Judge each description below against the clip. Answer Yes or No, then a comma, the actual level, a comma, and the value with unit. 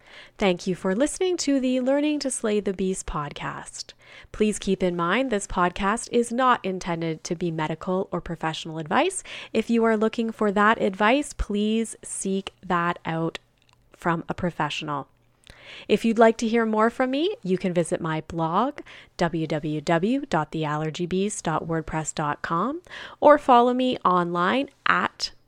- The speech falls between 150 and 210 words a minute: No, average, 140 wpm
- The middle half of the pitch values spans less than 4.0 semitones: No, wide, 5.6 semitones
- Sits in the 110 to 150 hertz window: No, high, 190 Hz